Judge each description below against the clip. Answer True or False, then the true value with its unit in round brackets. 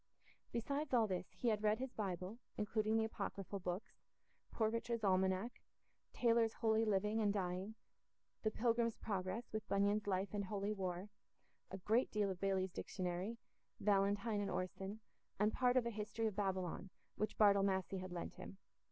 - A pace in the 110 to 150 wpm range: False (160 wpm)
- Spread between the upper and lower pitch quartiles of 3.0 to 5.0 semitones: False (2.6 semitones)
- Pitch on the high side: True (205 Hz)